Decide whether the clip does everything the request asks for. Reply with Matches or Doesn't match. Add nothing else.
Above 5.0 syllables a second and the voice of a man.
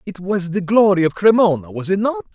Matches